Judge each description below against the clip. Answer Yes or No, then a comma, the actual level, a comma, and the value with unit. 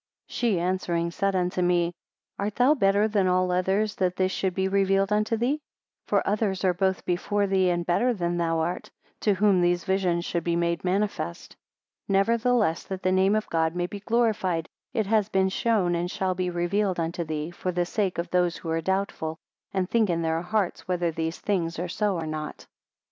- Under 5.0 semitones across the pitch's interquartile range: Yes, narrow, 2.6 semitones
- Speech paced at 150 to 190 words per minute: No, average, 200 wpm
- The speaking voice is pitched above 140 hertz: Yes, medium, 185 Hz